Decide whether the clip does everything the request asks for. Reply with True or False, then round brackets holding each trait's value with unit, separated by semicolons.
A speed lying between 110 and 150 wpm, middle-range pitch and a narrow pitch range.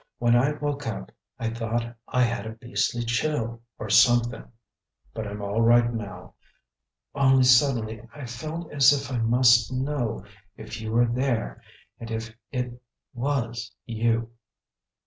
False (145 wpm; 120 Hz; 2.2 semitones)